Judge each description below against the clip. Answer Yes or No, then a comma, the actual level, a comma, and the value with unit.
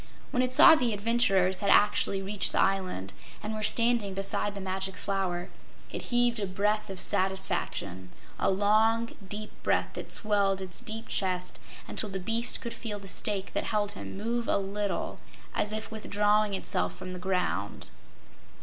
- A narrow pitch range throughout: Yes, narrow, 2.2 semitones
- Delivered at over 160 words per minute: Yes, average, 170 wpm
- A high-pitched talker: Yes, high, 205 Hz